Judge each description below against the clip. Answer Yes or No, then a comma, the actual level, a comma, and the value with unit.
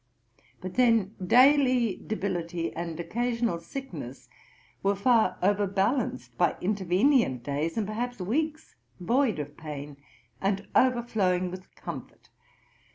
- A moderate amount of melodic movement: No, wide, 5.7 semitones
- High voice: Yes, high, 200 Hz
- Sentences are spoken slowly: Yes, slow, 105 wpm